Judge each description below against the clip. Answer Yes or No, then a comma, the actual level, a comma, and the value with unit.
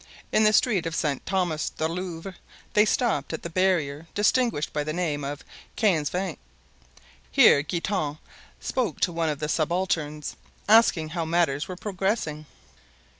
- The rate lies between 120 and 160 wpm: Yes, average, 150 wpm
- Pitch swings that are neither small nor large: Yes, average, 4.0 semitones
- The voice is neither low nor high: Yes, medium, 165 Hz